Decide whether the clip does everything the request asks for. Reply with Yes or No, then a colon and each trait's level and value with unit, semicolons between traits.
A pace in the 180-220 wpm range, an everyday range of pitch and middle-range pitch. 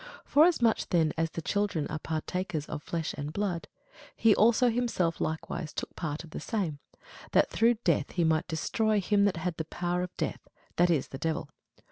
Yes: average, 185 wpm; average, 4.6 semitones; medium, 175 Hz